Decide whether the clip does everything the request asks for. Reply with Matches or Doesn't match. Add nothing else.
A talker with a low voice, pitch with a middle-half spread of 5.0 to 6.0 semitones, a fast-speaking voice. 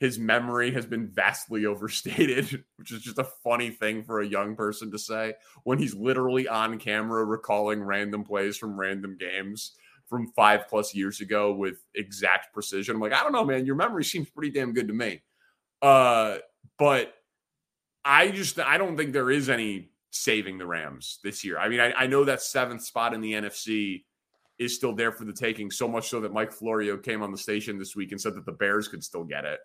Doesn't match